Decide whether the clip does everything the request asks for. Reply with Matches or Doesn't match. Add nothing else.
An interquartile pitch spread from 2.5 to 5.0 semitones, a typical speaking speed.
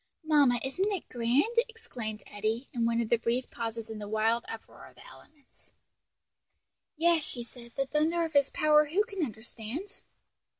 Doesn't match